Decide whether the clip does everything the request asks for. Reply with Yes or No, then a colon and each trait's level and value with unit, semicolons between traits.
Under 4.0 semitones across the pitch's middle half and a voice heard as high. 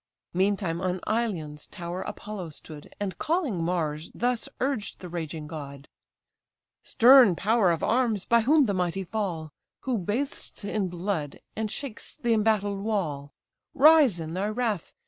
No: average, 5.1 semitones; high, 195 Hz